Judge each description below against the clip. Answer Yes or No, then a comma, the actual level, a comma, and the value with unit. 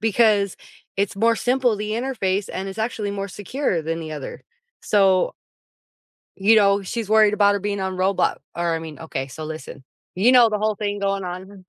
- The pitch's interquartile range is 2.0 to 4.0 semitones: Yes, average, 2.7 semitones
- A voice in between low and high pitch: No, high, 200 Hz